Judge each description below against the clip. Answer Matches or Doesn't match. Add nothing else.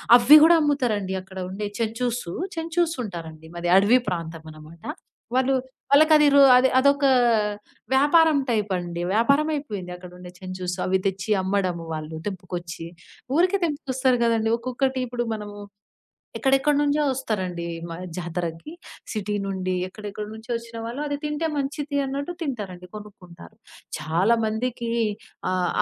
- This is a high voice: Matches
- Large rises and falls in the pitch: Matches